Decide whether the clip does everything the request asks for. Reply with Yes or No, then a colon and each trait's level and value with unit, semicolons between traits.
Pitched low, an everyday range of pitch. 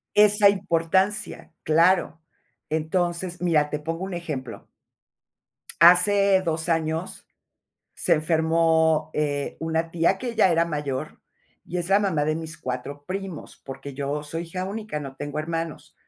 No: medium, 165 Hz; average, 3.2 semitones